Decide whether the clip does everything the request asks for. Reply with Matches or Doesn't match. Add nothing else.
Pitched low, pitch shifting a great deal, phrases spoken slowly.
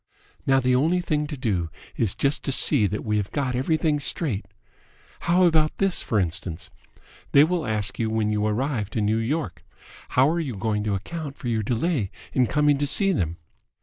Doesn't match